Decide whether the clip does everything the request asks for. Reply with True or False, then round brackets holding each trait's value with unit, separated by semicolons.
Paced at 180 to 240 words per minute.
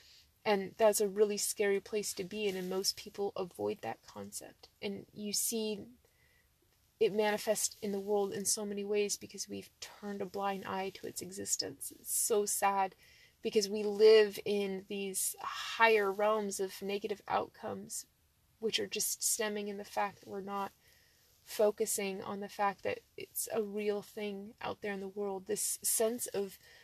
False (170 wpm)